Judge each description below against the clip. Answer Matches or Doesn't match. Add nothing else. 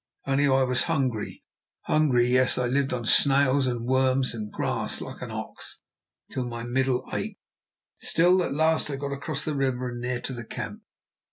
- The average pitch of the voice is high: Doesn't match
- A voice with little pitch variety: Matches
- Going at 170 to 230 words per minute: Matches